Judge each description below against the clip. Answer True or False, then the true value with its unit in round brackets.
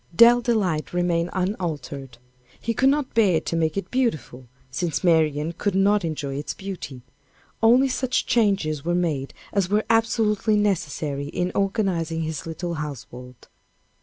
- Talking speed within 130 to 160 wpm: True (140 wpm)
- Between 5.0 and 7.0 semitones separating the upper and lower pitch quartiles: True (5.3 semitones)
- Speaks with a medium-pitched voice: True (175 Hz)